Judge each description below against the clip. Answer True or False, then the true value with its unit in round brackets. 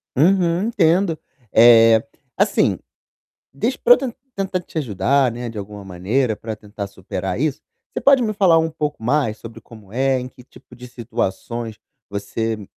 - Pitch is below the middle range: True (125 Hz)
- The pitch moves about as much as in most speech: False (6.9 semitones)